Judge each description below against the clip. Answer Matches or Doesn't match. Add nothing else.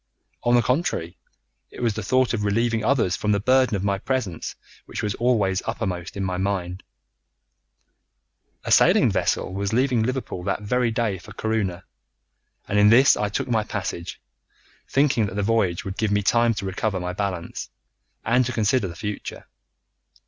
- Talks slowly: Doesn't match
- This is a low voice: Matches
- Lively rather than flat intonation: Doesn't match